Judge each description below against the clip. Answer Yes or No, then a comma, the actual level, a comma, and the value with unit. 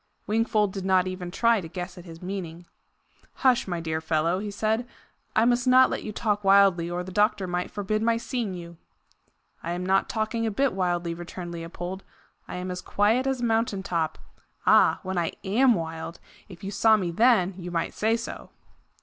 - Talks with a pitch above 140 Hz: Yes, high, 190 Hz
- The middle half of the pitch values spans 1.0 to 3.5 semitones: No, average, 3.9 semitones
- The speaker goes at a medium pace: Yes, average, 195 wpm